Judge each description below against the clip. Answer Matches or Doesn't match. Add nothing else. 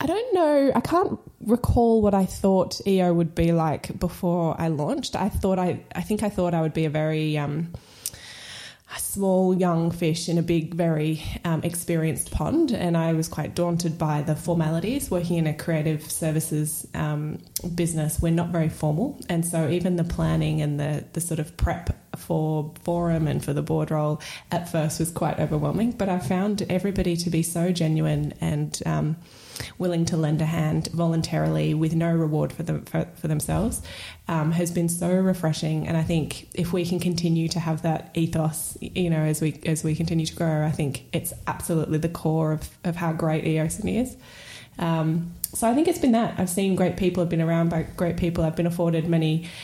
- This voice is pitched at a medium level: Matches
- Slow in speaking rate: Doesn't match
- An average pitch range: Doesn't match